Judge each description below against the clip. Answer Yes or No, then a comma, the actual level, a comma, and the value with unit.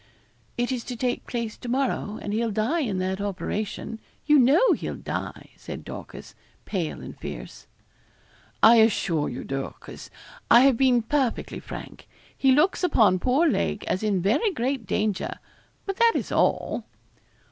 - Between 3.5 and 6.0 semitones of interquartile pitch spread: Yes, average, 4.8 semitones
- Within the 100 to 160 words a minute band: Yes, average, 155 wpm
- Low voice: No, high, 235 Hz